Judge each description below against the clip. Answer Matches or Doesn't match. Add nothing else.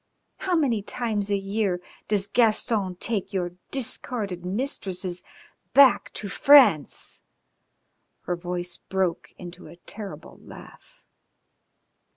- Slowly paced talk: Matches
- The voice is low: Doesn't match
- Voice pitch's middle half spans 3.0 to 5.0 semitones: Matches